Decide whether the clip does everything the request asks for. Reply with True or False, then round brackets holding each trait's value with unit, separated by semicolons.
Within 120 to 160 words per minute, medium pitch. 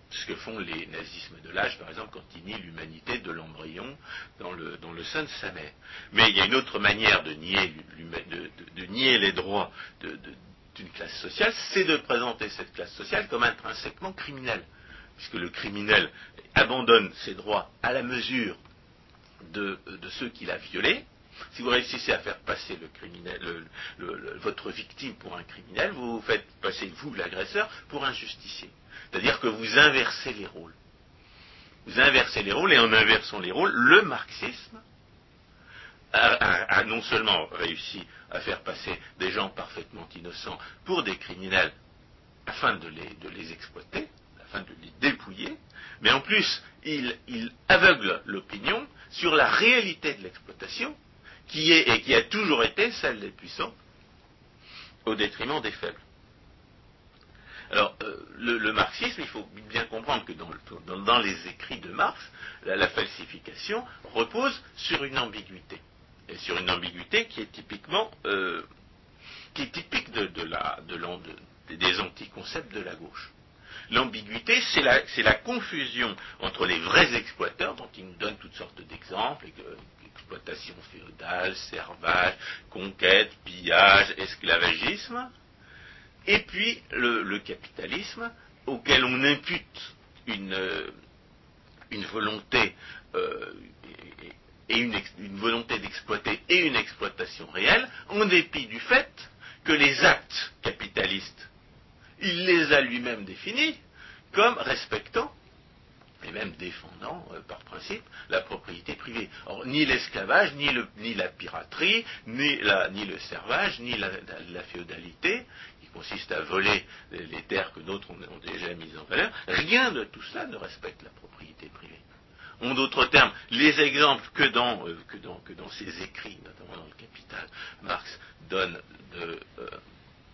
False (155 wpm; 125 Hz)